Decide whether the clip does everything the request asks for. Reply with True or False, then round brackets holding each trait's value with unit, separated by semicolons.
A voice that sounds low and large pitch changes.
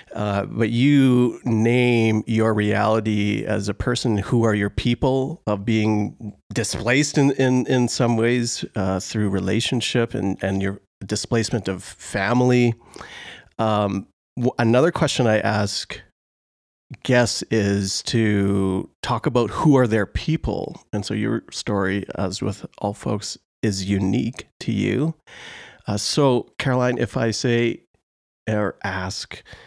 False (110 Hz; 3.5 semitones)